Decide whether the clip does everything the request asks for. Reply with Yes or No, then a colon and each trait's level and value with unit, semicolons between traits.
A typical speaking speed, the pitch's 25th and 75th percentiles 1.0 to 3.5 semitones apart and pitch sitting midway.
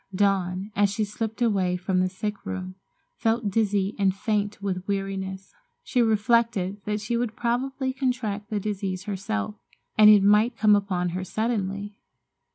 No: average, 155 wpm; narrow, 2.4 semitones; high, 205 Hz